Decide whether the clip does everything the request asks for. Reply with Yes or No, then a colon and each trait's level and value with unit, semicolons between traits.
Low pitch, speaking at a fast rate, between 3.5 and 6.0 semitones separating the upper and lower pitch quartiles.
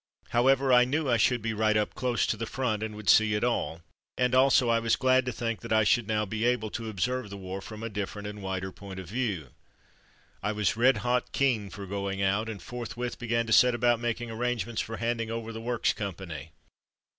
No: low, 115 Hz; fast, 225 wpm; average, 2.8 semitones